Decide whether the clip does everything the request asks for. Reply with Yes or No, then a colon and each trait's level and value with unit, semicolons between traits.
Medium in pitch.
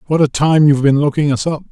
Yes: medium, 145 Hz